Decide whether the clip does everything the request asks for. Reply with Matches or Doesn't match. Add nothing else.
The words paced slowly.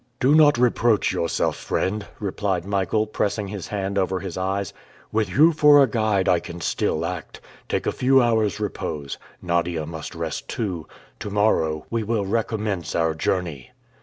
Doesn't match